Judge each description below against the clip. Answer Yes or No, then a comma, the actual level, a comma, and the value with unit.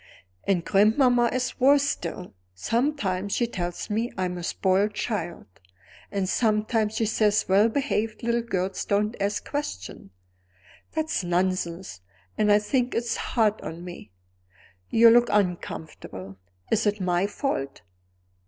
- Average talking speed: No, slow, 130 wpm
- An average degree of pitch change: Yes, average, 4.2 semitones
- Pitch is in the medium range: No, high, 210 Hz